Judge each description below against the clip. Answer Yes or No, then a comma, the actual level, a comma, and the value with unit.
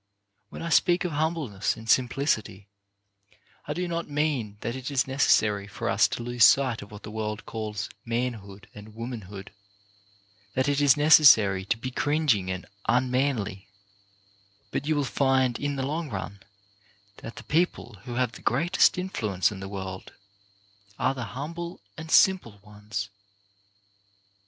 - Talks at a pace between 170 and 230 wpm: No, average, 150 wpm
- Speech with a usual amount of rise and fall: No, wide, 5.7 semitones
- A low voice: Yes, low, 120 Hz